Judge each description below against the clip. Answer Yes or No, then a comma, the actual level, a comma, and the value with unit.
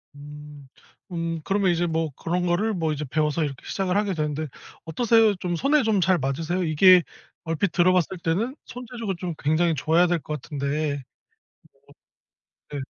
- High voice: No, medium, 170 Hz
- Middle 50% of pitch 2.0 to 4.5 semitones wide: Yes, average, 3.7 semitones